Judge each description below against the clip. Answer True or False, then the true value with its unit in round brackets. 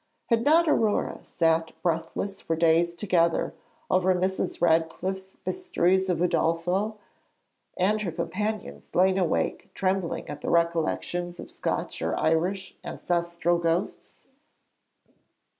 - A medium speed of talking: False (110 wpm)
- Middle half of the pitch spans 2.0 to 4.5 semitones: True (2.4 semitones)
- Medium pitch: True (175 Hz)